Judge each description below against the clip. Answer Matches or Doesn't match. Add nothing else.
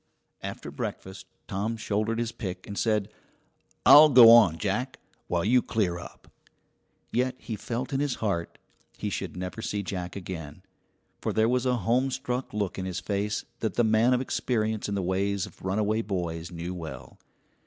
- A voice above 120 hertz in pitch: Doesn't match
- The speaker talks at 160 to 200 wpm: Matches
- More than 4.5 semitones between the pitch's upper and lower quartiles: Doesn't match